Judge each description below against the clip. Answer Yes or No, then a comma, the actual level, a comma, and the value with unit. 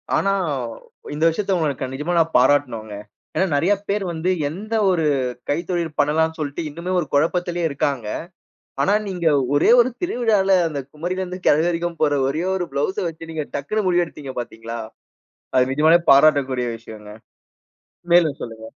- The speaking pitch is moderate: Yes, medium, 160 Hz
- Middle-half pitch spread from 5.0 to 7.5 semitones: No, average, 4.0 semitones